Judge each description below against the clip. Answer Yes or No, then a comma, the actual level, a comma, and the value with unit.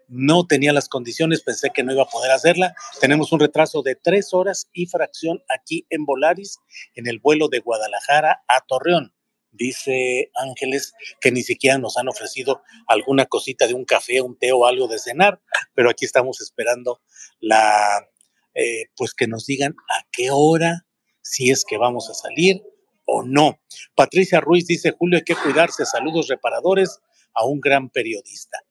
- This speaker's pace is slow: No, average, 170 wpm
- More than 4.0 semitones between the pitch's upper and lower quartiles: Yes, average, 4.9 semitones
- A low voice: No, medium, 145 Hz